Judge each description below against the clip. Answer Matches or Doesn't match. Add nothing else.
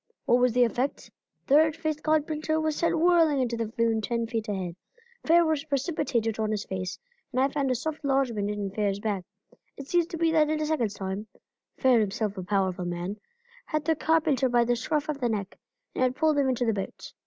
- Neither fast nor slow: Doesn't match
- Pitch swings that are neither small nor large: Doesn't match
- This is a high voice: Matches